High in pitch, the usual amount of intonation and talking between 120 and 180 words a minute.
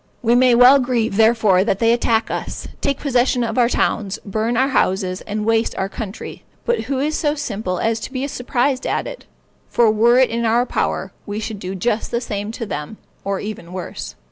No: high, 230 Hz; average, 3.3 semitones; fast, 205 wpm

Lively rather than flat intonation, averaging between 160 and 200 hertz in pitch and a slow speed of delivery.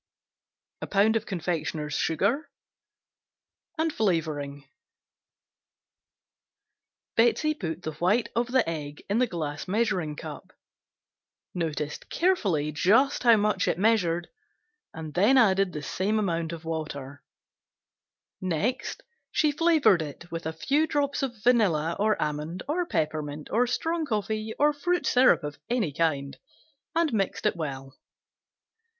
Yes: wide, 7.2 semitones; medium, 185 Hz; slow, 120 wpm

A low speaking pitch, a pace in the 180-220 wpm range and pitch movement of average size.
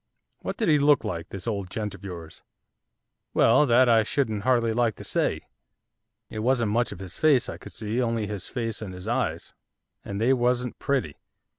Yes: low, 115 Hz; average, 190 wpm; average, 3.7 semitones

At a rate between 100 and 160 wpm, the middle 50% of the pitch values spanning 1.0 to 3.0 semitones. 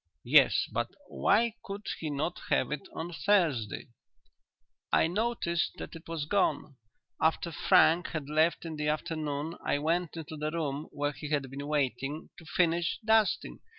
Yes: average, 155 wpm; average, 2.7 semitones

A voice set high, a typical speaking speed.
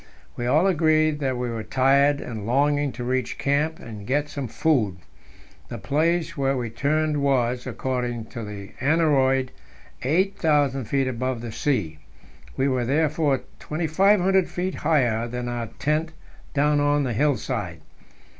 No: medium, 140 Hz; average, 145 wpm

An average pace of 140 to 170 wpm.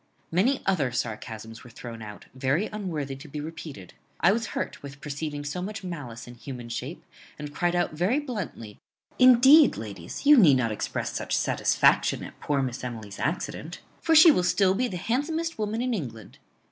No: average, 180 wpm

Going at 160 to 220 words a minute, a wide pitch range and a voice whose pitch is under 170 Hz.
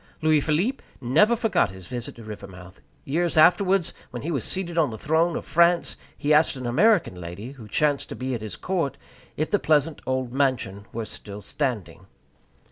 Yes: average, 185 wpm; wide, 6.6 semitones; medium, 140 Hz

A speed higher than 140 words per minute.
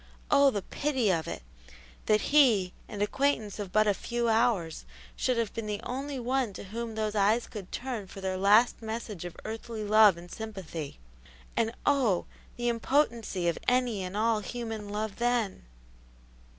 Yes: average, 165 wpm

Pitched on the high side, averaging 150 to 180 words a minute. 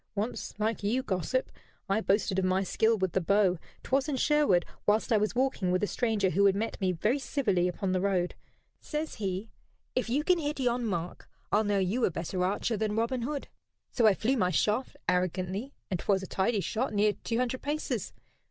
No: high, 210 Hz; fast, 205 wpm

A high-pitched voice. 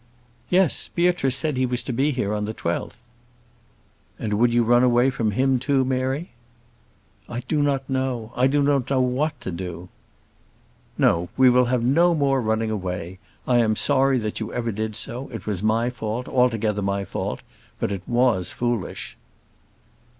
No: low, 120 Hz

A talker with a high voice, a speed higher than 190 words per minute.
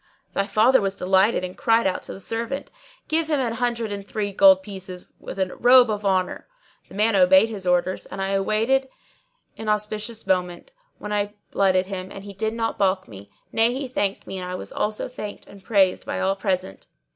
Yes: high, 200 Hz; fast, 205 wpm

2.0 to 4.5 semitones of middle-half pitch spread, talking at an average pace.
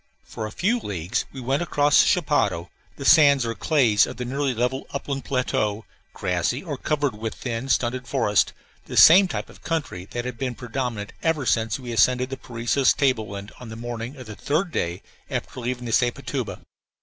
Yes: average, 3.8 semitones; average, 190 wpm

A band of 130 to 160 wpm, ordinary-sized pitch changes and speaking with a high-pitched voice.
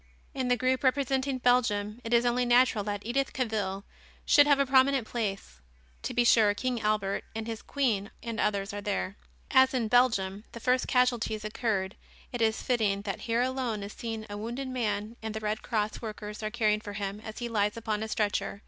No: average, 200 wpm; average, 3.1 semitones; high, 225 Hz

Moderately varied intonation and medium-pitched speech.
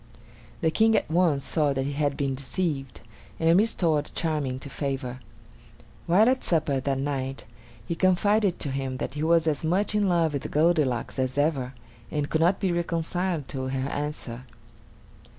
Yes: average, 4.1 semitones; medium, 150 Hz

